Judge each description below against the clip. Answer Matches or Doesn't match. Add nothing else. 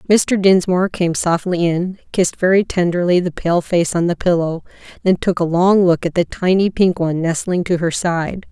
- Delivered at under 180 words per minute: Doesn't match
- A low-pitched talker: Doesn't match